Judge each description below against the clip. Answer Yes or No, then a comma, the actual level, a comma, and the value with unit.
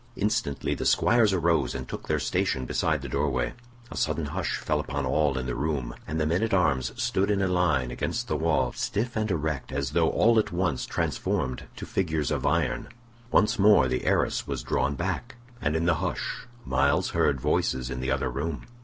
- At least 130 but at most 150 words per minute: No, fast, 205 wpm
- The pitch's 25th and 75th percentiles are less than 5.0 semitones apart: No, average, 5.3 semitones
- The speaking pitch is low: Yes, very low, 75 Hz